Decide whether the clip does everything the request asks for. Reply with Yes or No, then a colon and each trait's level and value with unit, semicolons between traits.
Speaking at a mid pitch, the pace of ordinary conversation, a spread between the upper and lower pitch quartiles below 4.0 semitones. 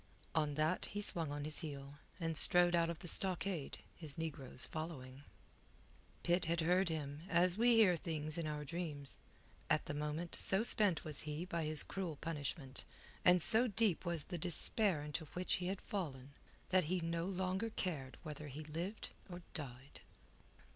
Yes: medium, 165 Hz; average, 170 wpm; average, 3.3 semitones